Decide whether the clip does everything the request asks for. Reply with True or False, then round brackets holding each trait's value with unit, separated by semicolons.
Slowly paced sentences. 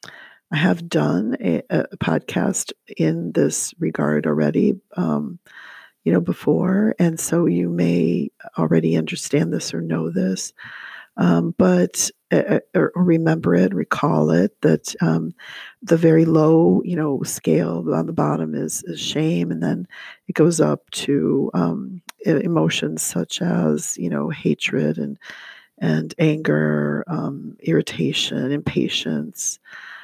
True (130 wpm)